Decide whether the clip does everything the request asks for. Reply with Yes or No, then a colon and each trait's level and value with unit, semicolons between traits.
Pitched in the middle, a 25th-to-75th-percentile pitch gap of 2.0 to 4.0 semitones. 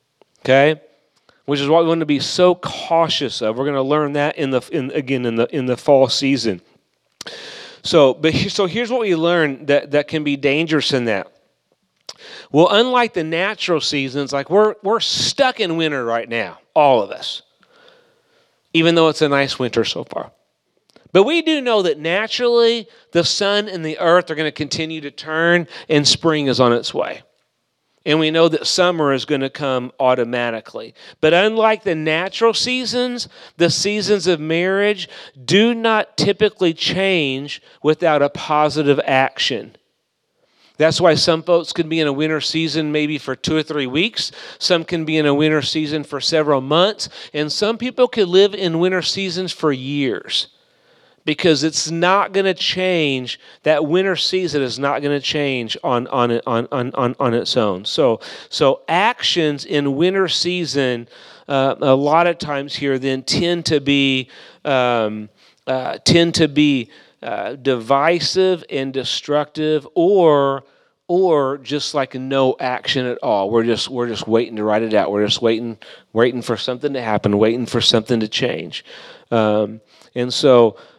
No: medium, 150 Hz; average, 4.8 semitones